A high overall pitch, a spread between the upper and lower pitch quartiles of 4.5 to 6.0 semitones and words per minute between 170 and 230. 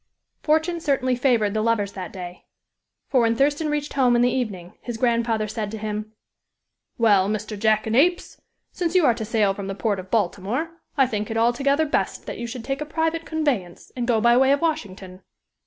Yes: high, 235 Hz; average, 4.8 semitones; average, 195 wpm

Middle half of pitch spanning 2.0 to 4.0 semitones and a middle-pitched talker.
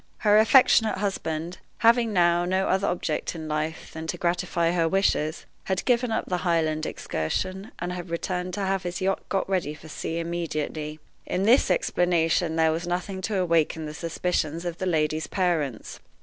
Yes: average, 2.9 semitones; medium, 175 Hz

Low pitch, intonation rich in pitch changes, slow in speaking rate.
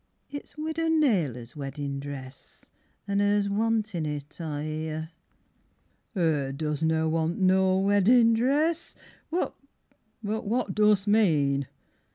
No: medium, 185 Hz; wide, 6.5 semitones; slow, 110 wpm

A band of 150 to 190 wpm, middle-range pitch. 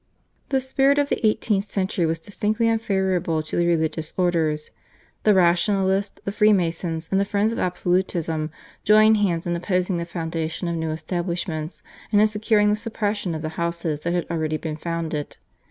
Yes: average, 170 wpm; medium, 175 Hz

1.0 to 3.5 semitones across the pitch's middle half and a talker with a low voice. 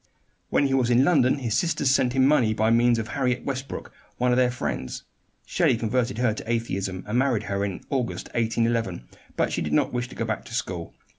Yes: average, 2.8 semitones; low, 120 Hz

